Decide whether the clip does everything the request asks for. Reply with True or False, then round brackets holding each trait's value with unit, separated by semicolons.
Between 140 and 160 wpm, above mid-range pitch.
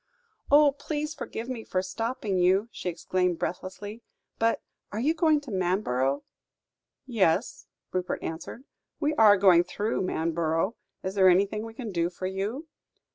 True (145 wpm; 195 Hz)